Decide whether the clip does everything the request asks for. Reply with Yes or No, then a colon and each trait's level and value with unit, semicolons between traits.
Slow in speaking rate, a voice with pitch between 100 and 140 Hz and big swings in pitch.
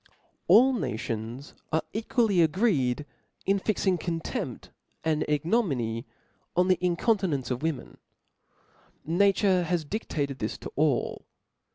No: slow, 110 wpm; medium, 165 Hz; wide, 5.8 semitones